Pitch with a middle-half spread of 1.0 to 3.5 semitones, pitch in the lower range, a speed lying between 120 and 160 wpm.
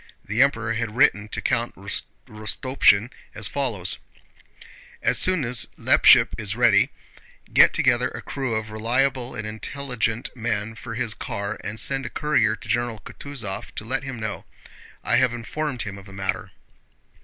Yes: average, 3.2 semitones; low, 115 Hz; average, 155 wpm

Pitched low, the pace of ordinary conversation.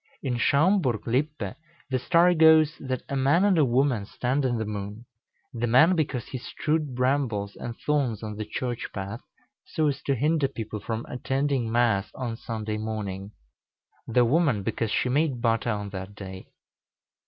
Yes: low, 125 Hz; average, 165 wpm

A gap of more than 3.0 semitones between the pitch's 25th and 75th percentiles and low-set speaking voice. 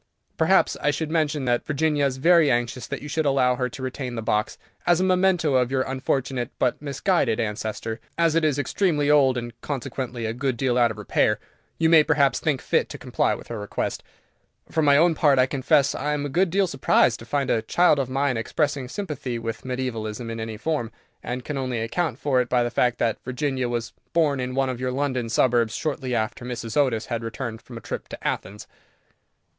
Yes: average, 3.6 semitones; low, 130 Hz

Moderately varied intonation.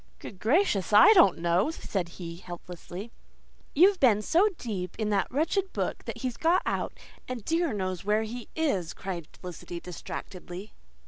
No: wide, 8.0 semitones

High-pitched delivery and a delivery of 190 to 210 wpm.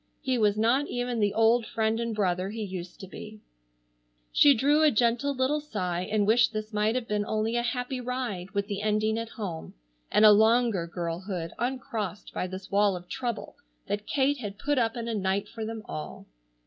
Yes: high, 220 Hz; average, 200 wpm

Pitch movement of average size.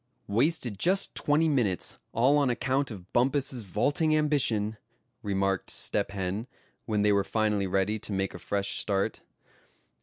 No: wide, 5.7 semitones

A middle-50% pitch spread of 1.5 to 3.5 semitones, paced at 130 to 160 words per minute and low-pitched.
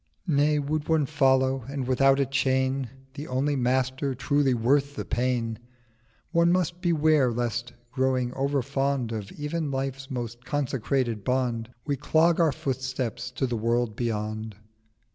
Yes: average, 2.8 semitones; average, 145 wpm; low, 130 Hz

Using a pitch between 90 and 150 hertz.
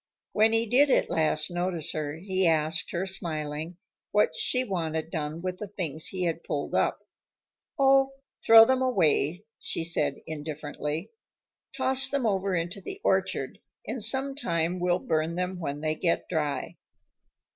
No: medium, 175 Hz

